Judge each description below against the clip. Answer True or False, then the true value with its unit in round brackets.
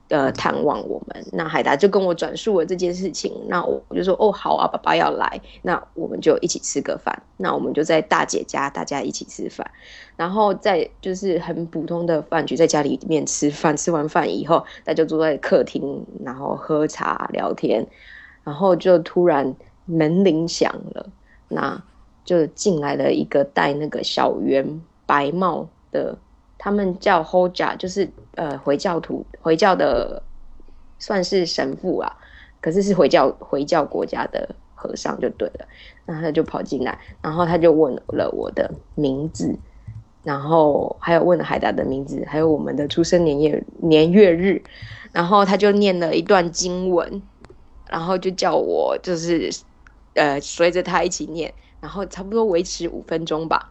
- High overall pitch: False (170 Hz)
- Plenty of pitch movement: False (3.1 semitones)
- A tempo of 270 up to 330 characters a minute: False (245 characters per minute)